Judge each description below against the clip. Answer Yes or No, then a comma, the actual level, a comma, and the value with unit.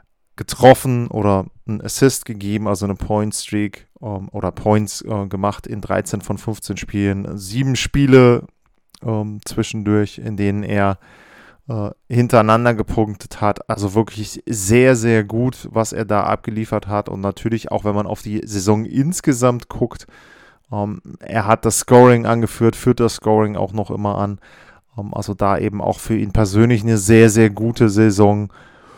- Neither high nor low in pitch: No, low, 110 Hz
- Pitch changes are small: Yes, narrow, 1.9 semitones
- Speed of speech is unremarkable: Yes, average, 145 wpm